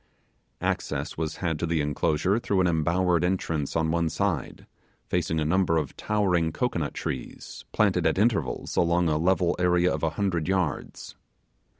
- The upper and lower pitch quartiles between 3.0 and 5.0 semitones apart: No, narrow, 2.5 semitones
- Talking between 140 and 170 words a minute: Yes, average, 160 wpm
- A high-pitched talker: No, very low, 85 Hz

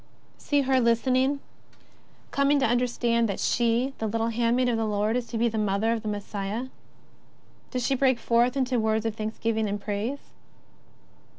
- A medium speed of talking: Yes, average, 175 wpm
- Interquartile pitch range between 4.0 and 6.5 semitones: No, narrow, 2.5 semitones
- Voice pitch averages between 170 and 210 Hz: No, high, 230 Hz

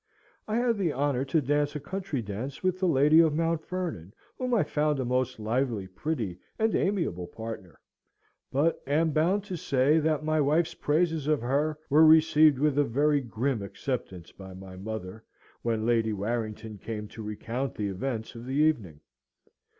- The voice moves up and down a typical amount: No, wide, 6.0 semitones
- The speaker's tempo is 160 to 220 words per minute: Yes, average, 175 wpm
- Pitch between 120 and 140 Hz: Yes, low, 135 Hz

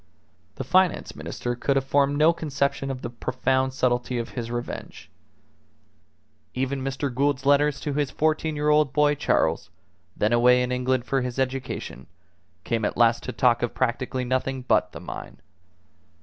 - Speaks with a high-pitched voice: No, low, 130 Hz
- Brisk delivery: No, average, 165 wpm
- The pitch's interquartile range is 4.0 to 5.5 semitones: No, narrow, 2.5 semitones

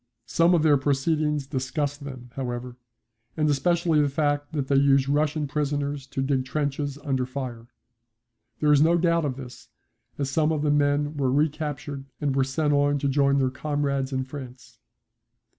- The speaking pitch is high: No, medium, 145 Hz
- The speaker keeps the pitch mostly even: Yes, narrow, 2.0 semitones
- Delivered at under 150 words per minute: No, average, 170 wpm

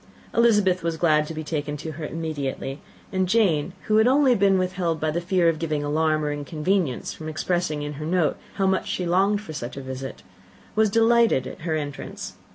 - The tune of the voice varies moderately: Yes, average, 4.1 semitones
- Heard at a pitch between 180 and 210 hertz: No, medium, 165 Hz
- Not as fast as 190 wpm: No, average, 200 wpm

